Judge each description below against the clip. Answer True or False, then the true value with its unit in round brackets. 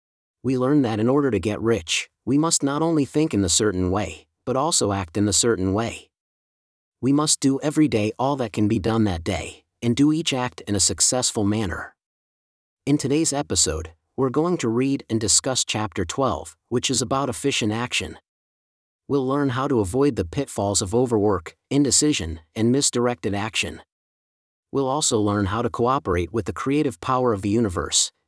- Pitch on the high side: False (115 Hz)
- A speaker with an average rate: True (180 wpm)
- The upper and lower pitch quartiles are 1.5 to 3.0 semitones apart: False (5.3 semitones)